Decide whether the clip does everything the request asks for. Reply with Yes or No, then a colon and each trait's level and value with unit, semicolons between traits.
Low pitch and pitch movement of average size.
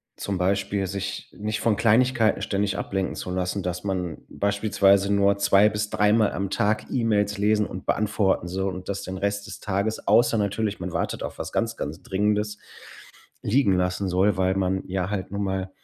No: low, 100 Hz; narrow, 1.8 semitones